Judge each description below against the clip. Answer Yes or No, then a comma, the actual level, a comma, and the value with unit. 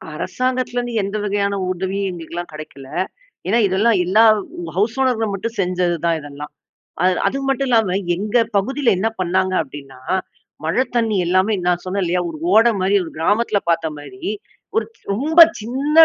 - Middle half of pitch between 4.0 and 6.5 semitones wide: Yes, average, 5.0 semitones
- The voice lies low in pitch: No, high, 200 Hz